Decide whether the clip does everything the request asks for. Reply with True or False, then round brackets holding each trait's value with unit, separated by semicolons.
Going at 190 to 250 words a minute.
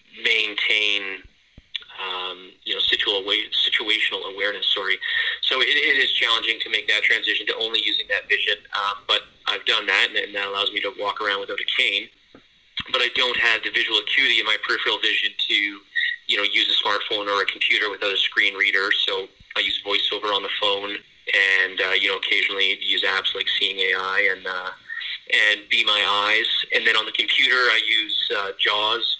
True (195 wpm)